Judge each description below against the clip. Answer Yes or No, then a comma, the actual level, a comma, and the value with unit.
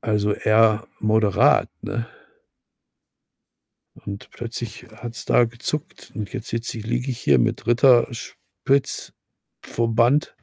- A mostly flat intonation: Yes, narrow, 2.0 semitones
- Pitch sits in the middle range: No, low, 115 Hz